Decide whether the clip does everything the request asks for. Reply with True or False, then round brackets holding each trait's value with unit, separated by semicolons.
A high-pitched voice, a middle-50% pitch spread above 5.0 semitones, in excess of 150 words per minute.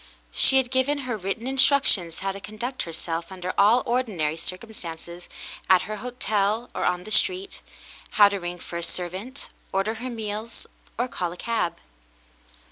True (210 Hz; 5.5 semitones; 165 wpm)